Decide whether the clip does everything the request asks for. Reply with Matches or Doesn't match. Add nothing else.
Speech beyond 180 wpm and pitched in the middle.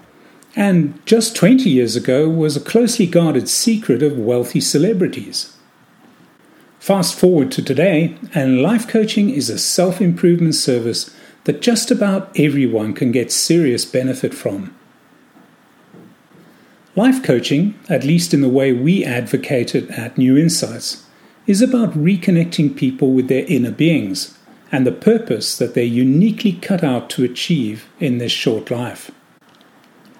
Doesn't match